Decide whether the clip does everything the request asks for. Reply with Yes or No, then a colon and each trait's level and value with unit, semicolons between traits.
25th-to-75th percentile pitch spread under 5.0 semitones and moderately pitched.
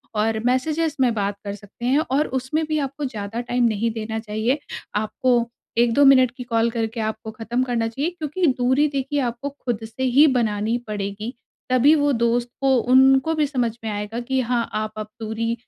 No: average, 3.3 semitones; high, 240 Hz